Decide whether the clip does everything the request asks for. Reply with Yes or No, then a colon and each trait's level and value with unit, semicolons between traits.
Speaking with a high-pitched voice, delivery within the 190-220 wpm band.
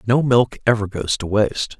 No: low, 110 Hz; average, 200 wpm